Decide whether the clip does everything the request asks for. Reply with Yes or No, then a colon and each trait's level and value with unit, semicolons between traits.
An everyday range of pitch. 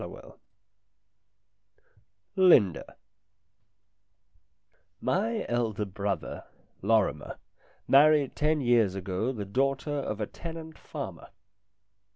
No: wide, 6.9 semitones